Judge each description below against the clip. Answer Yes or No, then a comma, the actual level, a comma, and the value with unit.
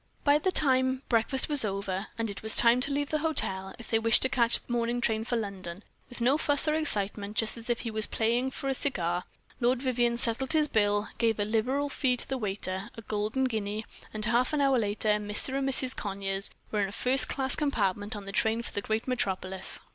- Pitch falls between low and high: No, high, 230 Hz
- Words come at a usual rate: No, fast, 225 wpm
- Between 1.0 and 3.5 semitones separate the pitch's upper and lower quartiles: No, average, 4.1 semitones